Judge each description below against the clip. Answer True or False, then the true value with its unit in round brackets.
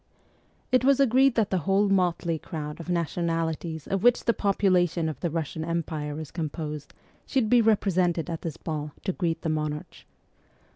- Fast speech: False (165 wpm)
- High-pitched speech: False (170 Hz)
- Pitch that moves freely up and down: False (3.7 semitones)